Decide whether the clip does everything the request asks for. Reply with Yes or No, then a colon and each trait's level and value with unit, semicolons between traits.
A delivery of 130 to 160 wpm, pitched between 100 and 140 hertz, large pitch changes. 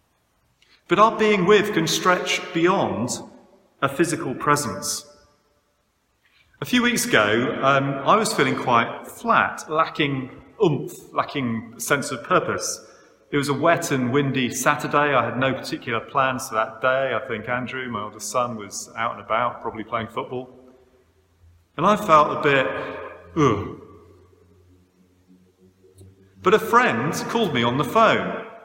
Yes: average, 140 wpm; low, 135 Hz; wide, 7.6 semitones